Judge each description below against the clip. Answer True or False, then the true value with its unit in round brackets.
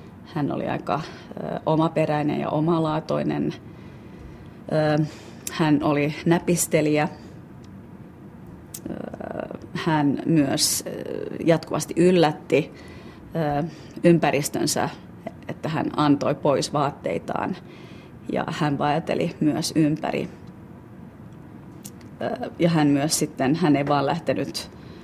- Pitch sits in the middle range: True (150 Hz)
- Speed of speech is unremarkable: False (75 wpm)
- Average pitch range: False (2.0 semitones)